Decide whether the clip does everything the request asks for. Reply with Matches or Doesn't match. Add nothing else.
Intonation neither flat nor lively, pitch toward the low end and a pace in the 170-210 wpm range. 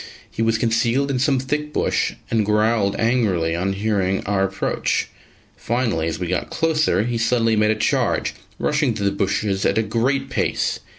Matches